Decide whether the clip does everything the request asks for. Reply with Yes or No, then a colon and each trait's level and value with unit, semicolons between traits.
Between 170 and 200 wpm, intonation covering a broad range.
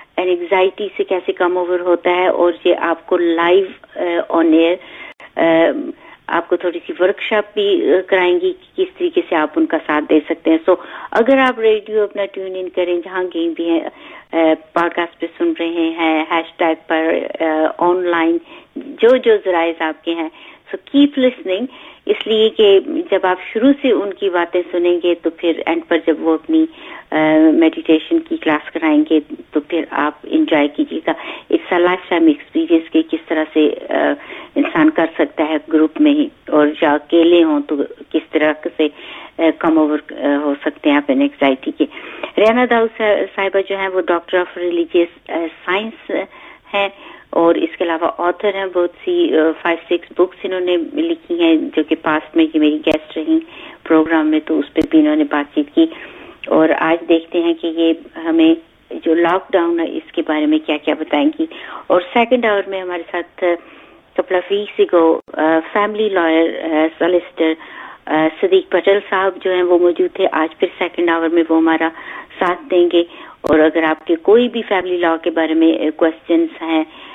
Yes: average, 180 wpm; wide, 6.2 semitones